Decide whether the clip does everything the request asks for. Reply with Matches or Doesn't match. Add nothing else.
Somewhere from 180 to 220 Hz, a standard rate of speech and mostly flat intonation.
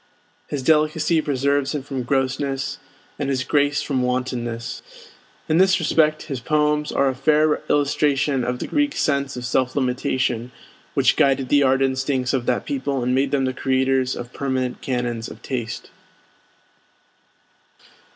Doesn't match